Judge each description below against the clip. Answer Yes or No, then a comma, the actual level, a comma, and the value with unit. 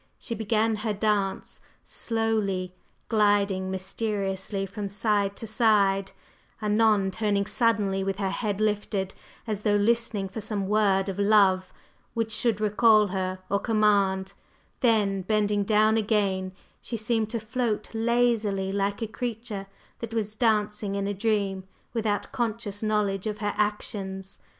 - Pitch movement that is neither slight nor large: No, narrow, 2.0 semitones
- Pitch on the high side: Yes, high, 210 Hz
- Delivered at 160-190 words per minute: No, slow, 135 wpm